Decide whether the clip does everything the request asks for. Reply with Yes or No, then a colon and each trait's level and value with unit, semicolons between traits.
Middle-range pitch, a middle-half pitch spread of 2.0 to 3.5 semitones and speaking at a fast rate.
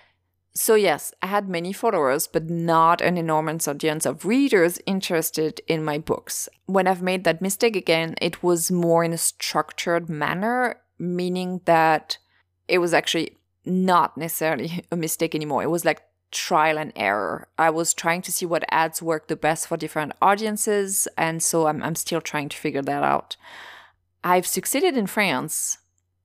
No: medium, 165 Hz; average, 2.7 semitones; average, 165 wpm